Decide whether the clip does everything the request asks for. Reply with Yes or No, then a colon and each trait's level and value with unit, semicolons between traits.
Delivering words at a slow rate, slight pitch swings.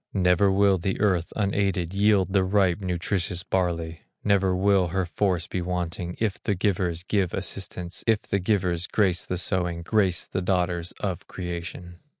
No: average, 155 wpm; narrow, 2.0 semitones